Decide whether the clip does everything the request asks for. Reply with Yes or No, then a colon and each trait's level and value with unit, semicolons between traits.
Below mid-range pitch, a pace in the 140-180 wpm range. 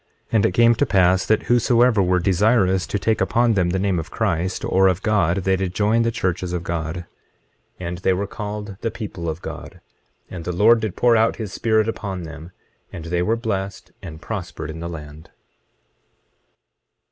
No: very low, 95 Hz; average, 195 wpm